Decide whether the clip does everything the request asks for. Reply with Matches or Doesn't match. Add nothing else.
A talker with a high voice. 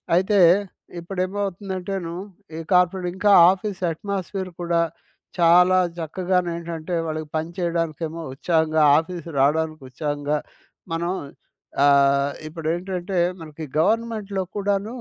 Doesn't match